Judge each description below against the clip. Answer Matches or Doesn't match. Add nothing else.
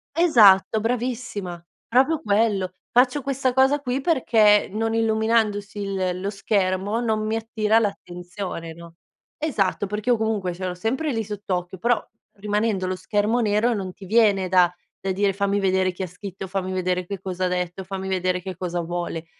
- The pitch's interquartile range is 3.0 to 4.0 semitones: Matches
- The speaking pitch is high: Matches